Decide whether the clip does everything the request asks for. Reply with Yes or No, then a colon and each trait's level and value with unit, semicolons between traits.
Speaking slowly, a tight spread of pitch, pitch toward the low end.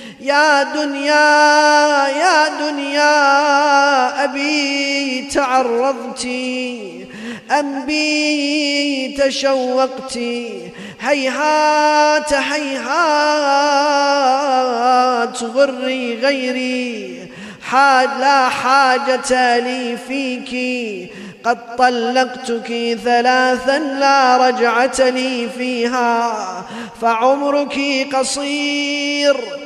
No: slow, 55 wpm; narrow, 2.3 semitones; very high, 265 Hz